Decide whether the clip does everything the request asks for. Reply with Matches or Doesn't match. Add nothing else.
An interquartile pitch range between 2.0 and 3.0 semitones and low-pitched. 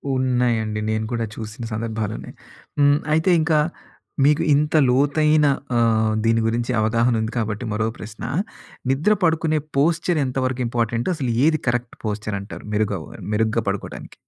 Doesn't match